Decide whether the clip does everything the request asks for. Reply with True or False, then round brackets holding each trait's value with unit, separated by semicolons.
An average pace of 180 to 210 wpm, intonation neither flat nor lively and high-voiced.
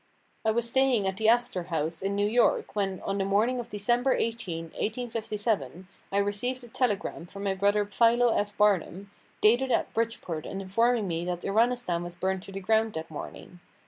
True (185 wpm; 3.5 semitones; 205 Hz)